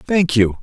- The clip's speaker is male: Yes, male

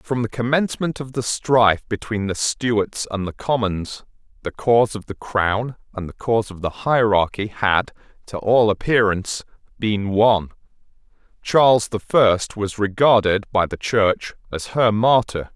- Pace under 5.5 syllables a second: Yes, 4.4 syllables/s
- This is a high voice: No, low, 110 Hz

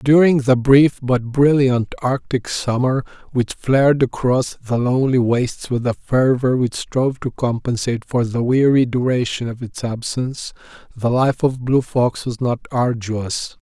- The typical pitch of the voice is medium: No, low, 125 Hz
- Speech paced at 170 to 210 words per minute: No, average, 155 wpm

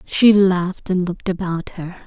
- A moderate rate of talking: Yes, average, 175 wpm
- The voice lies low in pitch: No, medium, 185 Hz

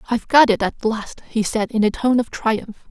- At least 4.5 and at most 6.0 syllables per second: Yes, 5.0 syllables/s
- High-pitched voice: Yes, high, 225 Hz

